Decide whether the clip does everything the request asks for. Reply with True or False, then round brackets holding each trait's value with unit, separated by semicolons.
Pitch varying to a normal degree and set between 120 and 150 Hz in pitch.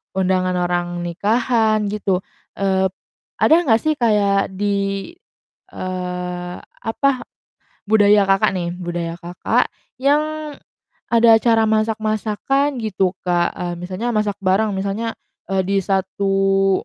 False (3.0 semitones; 200 Hz)